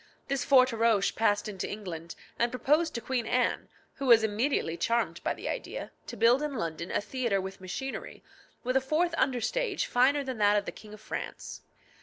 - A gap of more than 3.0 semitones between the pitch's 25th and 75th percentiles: Yes, average, 4.4 semitones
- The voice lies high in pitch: Yes, high, 235 Hz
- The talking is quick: No, average, 190 wpm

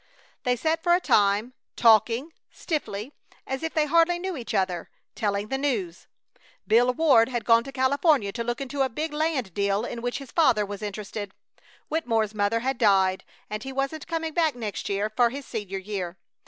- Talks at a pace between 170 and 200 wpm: Yes, average, 185 wpm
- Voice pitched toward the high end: Yes, high, 240 Hz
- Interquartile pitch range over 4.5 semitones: Yes, wide, 5.6 semitones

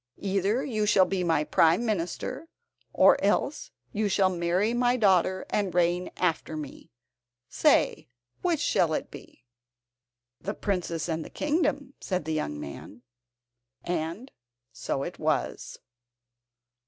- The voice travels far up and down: No, average, 4.5 semitones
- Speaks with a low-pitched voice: No, medium, 185 Hz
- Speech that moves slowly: Yes, slow, 130 wpm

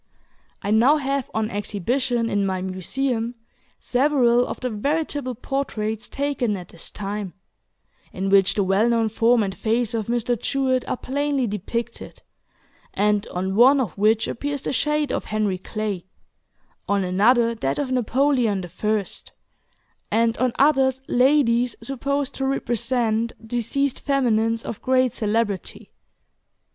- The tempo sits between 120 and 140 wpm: Yes, slow, 135 wpm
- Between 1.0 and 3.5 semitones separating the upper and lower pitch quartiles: No, average, 4.0 semitones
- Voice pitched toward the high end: Yes, high, 235 Hz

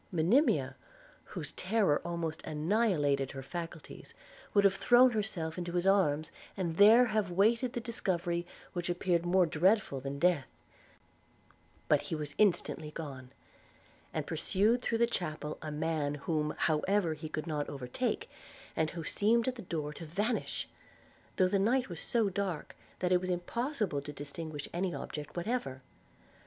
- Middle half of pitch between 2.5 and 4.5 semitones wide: No, average, 5.1 semitones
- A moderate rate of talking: Yes, average, 155 wpm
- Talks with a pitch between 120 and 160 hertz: No, medium, 175 Hz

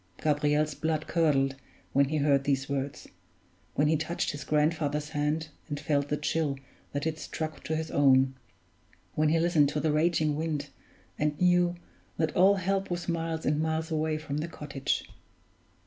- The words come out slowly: No, average, 165 wpm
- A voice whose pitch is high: No, medium, 155 Hz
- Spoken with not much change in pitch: Yes, narrow, 1.8 semitones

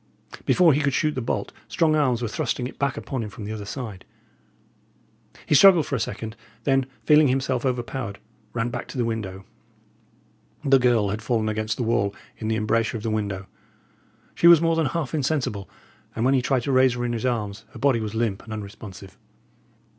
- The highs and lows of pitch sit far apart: No, average, 3.7 semitones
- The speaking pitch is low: Yes, low, 120 Hz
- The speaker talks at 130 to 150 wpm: No, average, 200 wpm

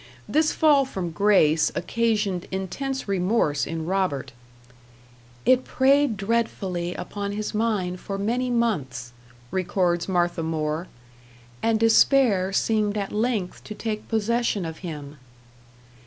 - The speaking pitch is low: No, high, 200 Hz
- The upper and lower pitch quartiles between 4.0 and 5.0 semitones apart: Yes, average, 4.6 semitones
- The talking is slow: Yes, slow, 115 wpm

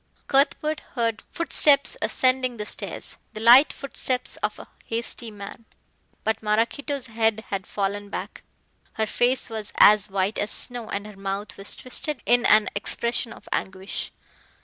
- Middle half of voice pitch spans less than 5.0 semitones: Yes, average, 3.6 semitones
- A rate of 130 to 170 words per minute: Yes, average, 150 wpm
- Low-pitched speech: No, high, 225 Hz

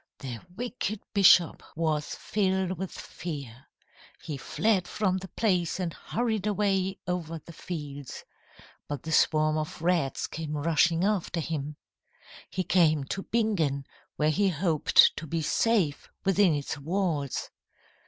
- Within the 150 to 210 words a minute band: No, slow, 135 wpm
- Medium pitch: Yes, medium, 170 Hz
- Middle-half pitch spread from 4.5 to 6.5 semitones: No, average, 4.1 semitones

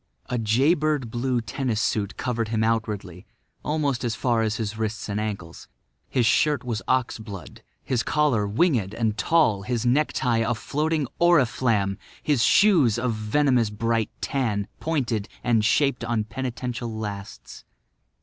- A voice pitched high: No, low, 115 Hz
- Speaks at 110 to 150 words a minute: Yes, average, 145 wpm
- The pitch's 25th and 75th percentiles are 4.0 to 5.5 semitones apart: No, average, 3.4 semitones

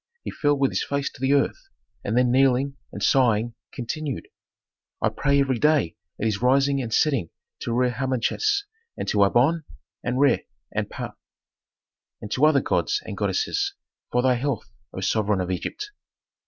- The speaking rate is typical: Yes, average, 165 wpm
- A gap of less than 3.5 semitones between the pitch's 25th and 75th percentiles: Yes, average, 3.1 semitones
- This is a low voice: Yes, low, 130 Hz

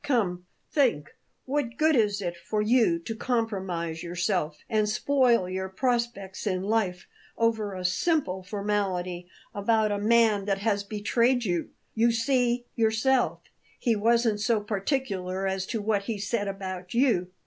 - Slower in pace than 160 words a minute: Yes, average, 145 wpm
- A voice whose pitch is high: Yes, high, 210 Hz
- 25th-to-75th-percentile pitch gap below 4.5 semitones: Yes, average, 3.7 semitones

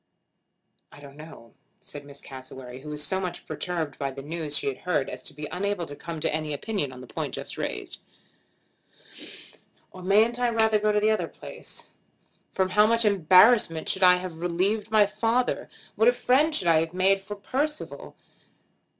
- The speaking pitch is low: No, medium, 180 Hz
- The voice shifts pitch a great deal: Yes, wide, 6.1 semitones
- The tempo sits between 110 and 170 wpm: No, average, 185 wpm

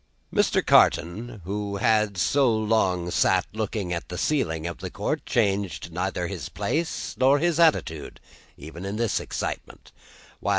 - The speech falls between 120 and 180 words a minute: Yes, average, 140 wpm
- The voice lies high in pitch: No, low, 100 Hz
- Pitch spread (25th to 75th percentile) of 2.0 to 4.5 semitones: No, average, 5.0 semitones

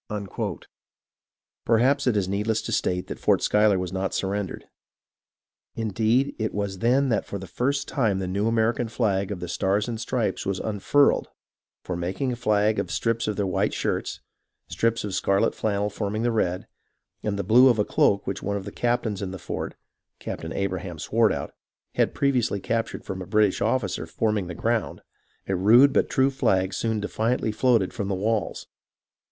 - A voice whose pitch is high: No, low, 105 Hz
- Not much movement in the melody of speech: No, average, 3.0 semitones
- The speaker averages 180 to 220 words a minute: Yes, average, 185 wpm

